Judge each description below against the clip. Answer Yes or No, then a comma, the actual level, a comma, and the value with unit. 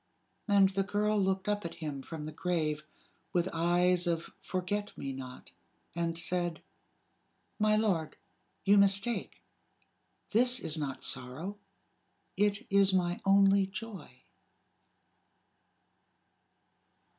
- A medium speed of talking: No, slow, 110 wpm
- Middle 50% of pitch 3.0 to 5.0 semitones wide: Yes, average, 3.5 semitones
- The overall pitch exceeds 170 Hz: Yes, medium, 185 Hz